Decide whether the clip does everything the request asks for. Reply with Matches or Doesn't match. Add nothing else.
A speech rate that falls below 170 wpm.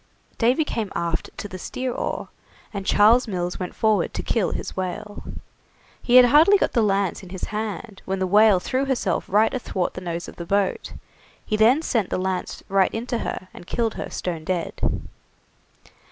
Doesn't match